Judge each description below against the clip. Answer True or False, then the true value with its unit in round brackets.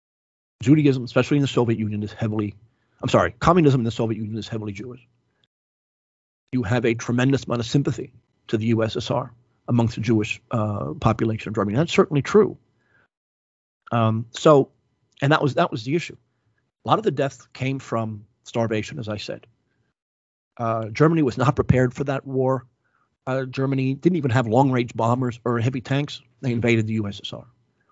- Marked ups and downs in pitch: False (3.2 semitones)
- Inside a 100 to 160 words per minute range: False (170 wpm)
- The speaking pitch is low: True (120 Hz)